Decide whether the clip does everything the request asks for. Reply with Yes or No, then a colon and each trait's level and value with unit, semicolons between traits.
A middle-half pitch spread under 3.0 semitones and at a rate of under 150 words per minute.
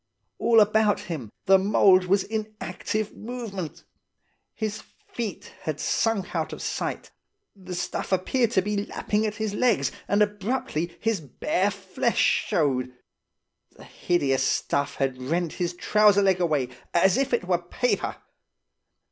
No: average, 3.7 semitones; average, 140 wpm